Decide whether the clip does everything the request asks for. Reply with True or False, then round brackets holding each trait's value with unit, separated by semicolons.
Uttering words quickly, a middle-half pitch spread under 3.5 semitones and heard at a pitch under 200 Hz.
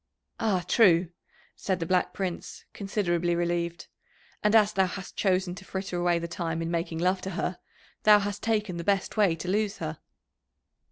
False (175 wpm; 2.8 semitones; 185 Hz)